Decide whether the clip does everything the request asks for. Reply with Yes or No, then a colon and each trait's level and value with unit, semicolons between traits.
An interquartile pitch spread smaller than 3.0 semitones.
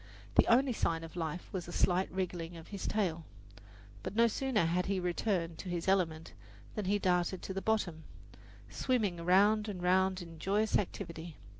No: average, 3.3 semitones